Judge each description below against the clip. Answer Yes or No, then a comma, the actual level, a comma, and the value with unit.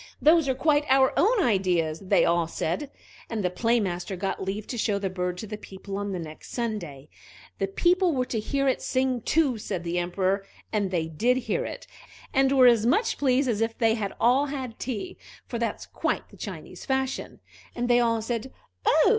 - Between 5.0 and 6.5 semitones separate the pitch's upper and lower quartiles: Yes, wide, 5.5 semitones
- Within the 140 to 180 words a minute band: No, fast, 205 wpm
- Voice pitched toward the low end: No, high, 230 Hz